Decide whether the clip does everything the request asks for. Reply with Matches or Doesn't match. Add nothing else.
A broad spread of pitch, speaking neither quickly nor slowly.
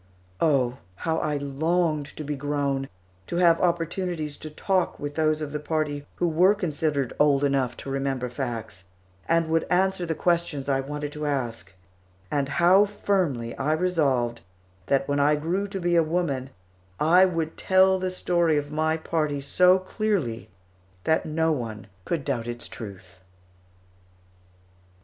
Doesn't match